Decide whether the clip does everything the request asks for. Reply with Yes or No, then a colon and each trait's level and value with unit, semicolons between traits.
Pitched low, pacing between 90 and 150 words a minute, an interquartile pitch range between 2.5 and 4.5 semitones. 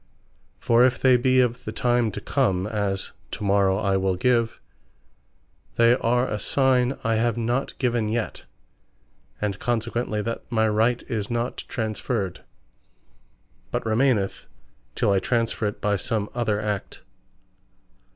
Yes: low, 115 Hz; average, 140 wpm; average, 2.8 semitones